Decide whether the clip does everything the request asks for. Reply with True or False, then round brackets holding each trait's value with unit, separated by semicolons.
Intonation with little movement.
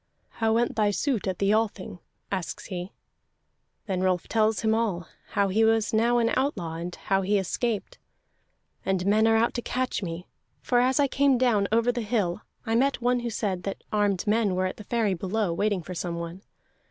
False (3.7 semitones)